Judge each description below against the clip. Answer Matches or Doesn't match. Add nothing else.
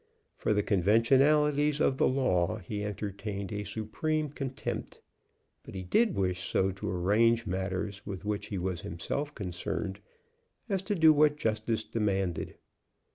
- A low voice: Matches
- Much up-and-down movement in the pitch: Matches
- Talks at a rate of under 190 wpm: Matches